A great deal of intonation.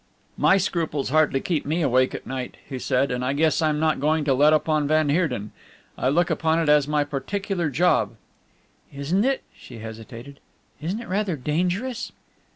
No: average, 3.9 semitones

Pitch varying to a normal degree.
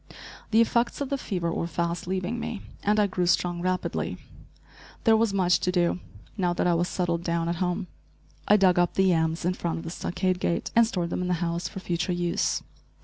No: narrow, 2.1 semitones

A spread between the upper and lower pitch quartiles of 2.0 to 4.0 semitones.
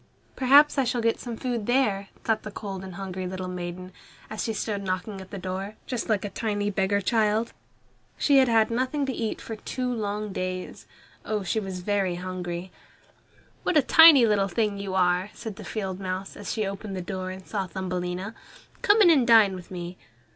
Yes: average, 3.5 semitones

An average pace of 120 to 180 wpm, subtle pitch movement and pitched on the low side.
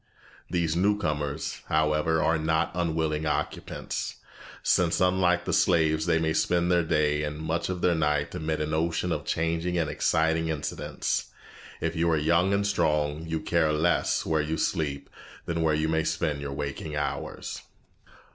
Yes: average, 165 wpm; narrow, 1.7 semitones; very low, 80 Hz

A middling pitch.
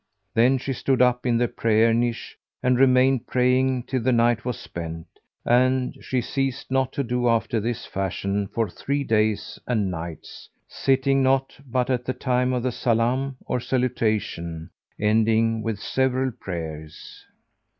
No: low, 120 Hz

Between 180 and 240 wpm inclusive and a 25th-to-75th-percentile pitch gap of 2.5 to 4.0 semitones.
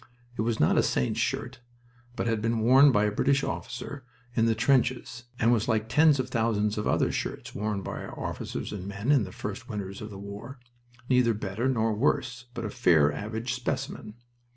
Yes: average, 200 wpm; average, 3.0 semitones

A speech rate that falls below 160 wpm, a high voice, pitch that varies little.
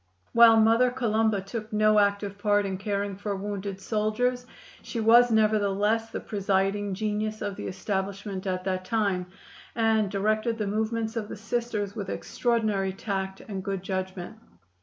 Yes: average, 150 wpm; high, 210 Hz; narrow, 2.2 semitones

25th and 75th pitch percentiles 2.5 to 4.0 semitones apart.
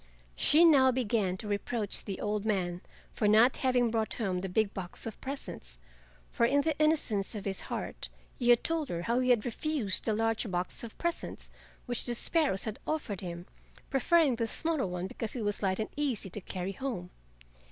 No: average, 5.0 semitones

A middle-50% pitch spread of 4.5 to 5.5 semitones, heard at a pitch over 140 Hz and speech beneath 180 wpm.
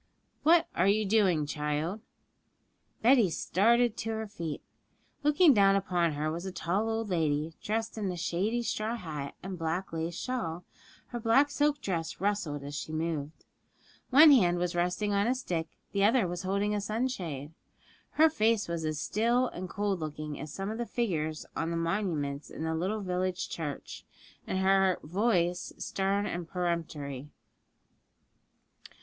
Yes: average, 5.0 semitones; medium, 185 Hz; average, 160 wpm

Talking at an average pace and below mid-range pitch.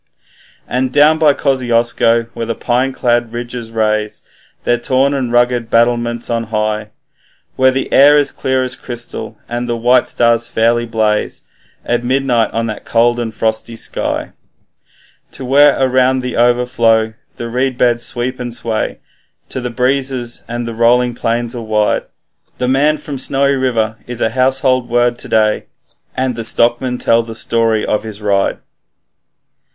Yes: average, 155 wpm; low, 120 Hz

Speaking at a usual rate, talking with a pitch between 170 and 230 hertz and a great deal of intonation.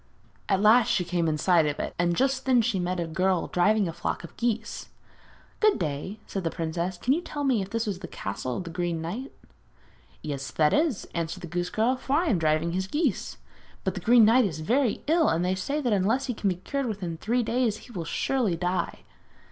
No: fast, 230 wpm; high, 190 Hz; wide, 6.1 semitones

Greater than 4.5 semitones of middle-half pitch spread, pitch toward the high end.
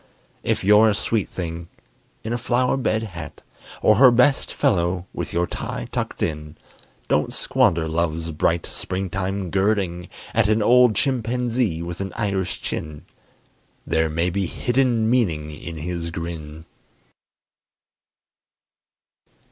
No: average, 5.1 semitones; very low, 95 Hz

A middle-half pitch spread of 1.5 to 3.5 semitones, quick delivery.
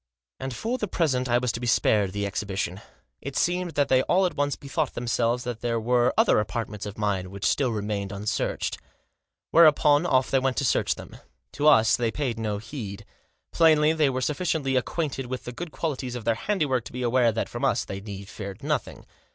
No: average, 5.1 semitones; fast, 210 wpm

